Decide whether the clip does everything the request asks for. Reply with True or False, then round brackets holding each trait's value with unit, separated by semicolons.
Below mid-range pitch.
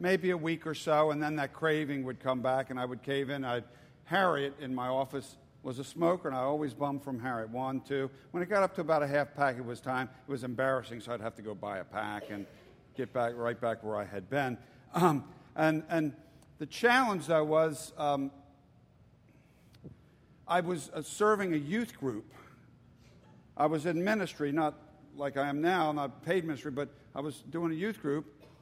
False (145 Hz)